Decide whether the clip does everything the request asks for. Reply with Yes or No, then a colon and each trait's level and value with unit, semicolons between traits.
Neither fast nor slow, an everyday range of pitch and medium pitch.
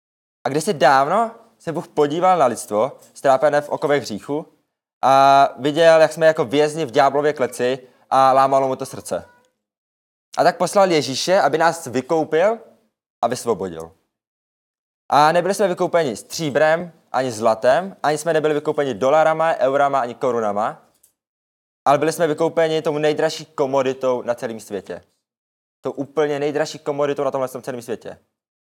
Yes: average, 145 wpm; average, 3.6 semitones; medium, 150 Hz